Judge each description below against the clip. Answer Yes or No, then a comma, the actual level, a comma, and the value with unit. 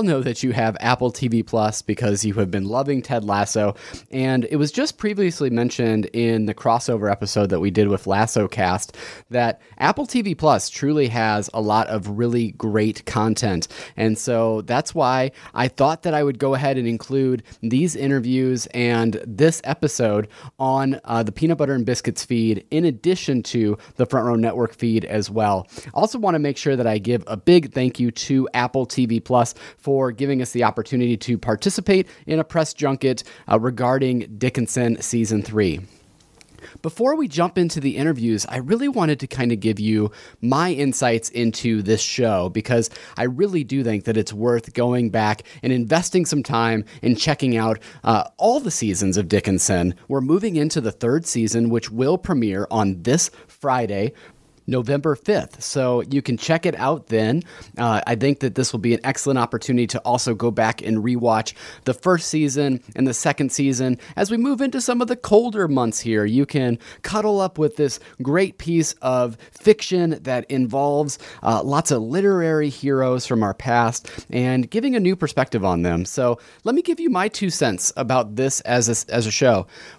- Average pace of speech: Yes, average, 185 wpm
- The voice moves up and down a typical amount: Yes, average, 4.5 semitones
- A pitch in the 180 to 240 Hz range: No, low, 125 Hz